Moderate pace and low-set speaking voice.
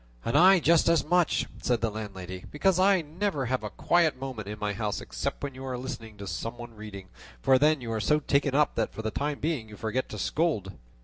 No: fast, 235 wpm; low, 130 Hz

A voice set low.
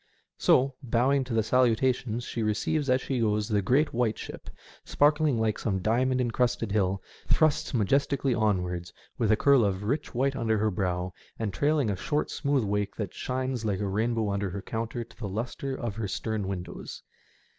Yes: low, 115 Hz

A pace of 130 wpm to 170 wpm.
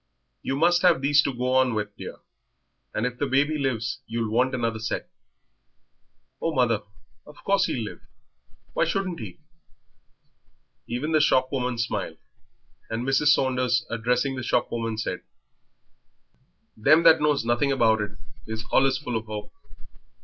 Yes: average, 145 wpm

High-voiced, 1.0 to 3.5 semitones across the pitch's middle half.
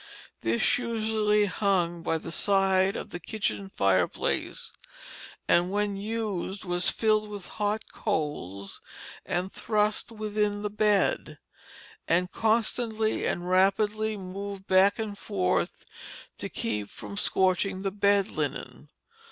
Yes: high, 200 Hz; average, 2.8 semitones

